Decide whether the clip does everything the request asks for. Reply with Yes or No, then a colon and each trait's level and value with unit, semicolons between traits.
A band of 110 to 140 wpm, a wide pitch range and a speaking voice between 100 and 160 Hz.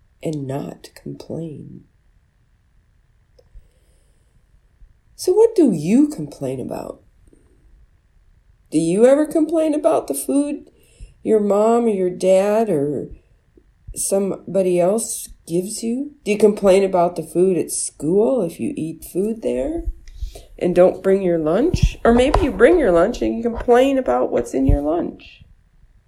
No: slow, 135 wpm; wide, 7.0 semitones; high, 195 Hz